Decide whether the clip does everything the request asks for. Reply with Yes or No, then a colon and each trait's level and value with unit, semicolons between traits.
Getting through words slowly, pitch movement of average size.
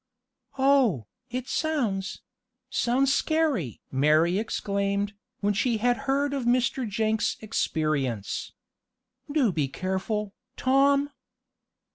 No: slow, 95 wpm; wide, 6.1 semitones